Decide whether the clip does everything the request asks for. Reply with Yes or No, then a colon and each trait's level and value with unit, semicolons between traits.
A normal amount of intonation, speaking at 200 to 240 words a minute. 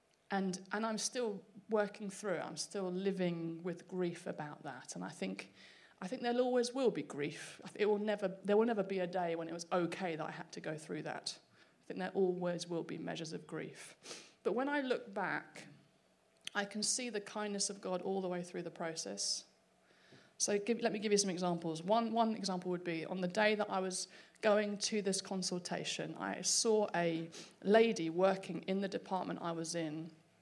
Yes: average, 3.1 semitones; fast, 205 wpm